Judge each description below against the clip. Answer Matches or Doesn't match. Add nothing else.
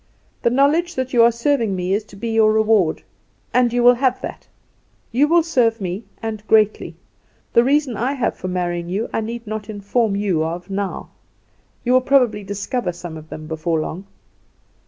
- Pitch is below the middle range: Doesn't match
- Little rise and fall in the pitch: Doesn't match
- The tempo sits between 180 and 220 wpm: Matches